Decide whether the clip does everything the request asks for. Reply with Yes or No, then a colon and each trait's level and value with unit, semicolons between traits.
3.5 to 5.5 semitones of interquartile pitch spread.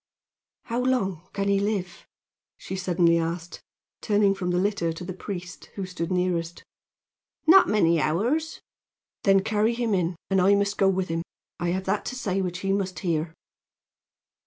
No: narrow, 2.5 semitones